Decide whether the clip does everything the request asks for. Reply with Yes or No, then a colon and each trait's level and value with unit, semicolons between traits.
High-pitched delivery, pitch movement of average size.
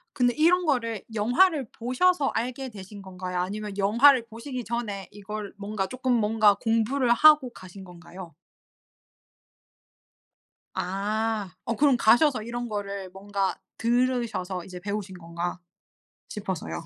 Yes: high, 215 Hz; average, 4.2 semitones